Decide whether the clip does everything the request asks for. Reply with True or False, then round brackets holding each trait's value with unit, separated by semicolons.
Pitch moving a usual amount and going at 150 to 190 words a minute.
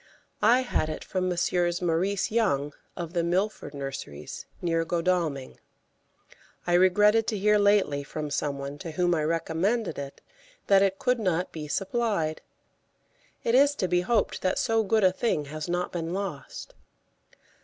True (4.5 semitones; 155 wpm)